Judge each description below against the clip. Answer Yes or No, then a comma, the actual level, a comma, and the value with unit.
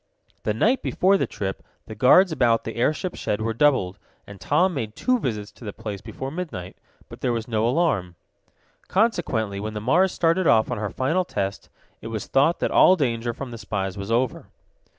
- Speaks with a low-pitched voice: Yes, low, 115 Hz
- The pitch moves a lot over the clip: Yes, wide, 7.3 semitones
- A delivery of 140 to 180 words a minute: No, average, 195 wpm